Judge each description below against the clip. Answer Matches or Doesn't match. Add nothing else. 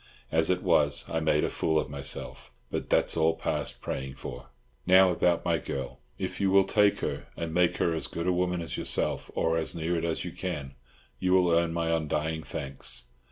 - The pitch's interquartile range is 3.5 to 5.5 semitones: Doesn't match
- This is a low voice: Matches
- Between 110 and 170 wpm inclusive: Doesn't match